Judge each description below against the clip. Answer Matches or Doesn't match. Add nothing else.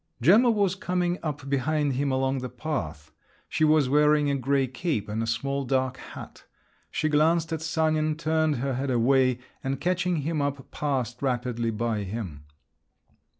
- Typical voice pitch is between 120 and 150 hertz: Matches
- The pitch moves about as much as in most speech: Matches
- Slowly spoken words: Doesn't match